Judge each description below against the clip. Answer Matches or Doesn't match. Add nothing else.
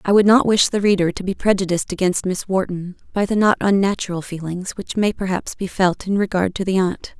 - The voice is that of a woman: Matches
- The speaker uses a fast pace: Matches